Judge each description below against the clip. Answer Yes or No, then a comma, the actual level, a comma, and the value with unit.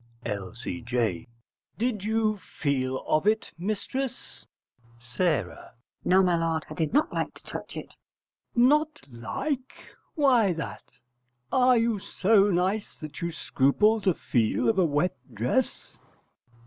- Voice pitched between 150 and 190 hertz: Yes, medium, 185 Hz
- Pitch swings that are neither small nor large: No, wide, 8.9 semitones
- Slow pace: Yes, slow, 130 wpm